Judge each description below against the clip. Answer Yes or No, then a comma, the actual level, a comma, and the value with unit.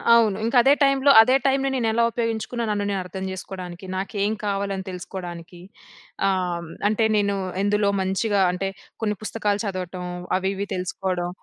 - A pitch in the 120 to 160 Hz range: No, high, 200 Hz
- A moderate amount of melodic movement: Yes, average, 3.0 semitones